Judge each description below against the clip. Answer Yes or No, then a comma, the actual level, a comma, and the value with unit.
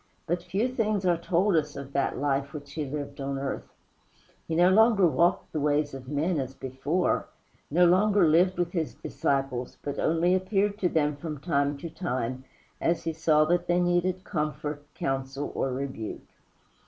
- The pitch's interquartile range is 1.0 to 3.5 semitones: No, average, 4.1 semitones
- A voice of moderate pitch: Yes, medium, 155 Hz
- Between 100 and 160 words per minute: No, average, 175 wpm